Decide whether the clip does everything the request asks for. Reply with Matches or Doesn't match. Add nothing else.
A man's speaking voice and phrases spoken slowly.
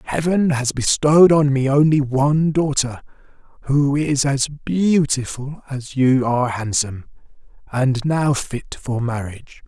Matches